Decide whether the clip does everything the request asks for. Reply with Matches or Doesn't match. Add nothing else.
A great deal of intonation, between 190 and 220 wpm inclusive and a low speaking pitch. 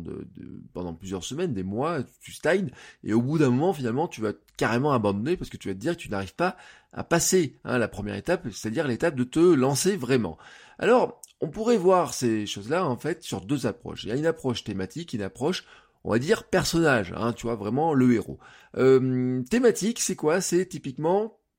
Matches